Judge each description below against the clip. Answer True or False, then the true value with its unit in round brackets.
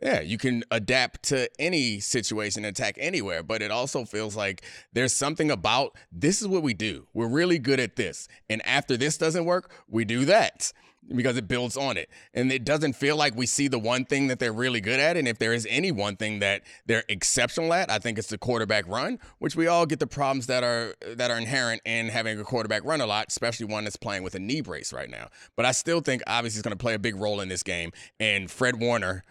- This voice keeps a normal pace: False (240 wpm)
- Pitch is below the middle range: True (120 Hz)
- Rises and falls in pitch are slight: False (4.1 semitones)